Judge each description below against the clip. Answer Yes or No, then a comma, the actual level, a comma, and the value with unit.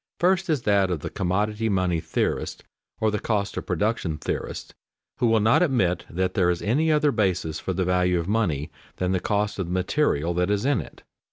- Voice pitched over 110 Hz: No, low, 100 Hz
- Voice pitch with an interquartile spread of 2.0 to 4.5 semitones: Yes, average, 4.0 semitones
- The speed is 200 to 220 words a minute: Yes, fast, 205 wpm